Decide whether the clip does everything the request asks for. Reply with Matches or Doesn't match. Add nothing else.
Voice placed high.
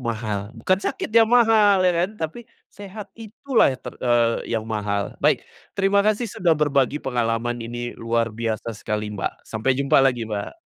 Doesn't match